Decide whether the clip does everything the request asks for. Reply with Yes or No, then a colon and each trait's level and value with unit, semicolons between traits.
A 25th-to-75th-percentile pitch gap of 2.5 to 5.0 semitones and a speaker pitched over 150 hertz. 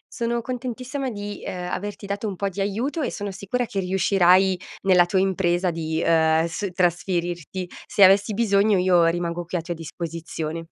Yes: average, 2.9 semitones; high, 190 Hz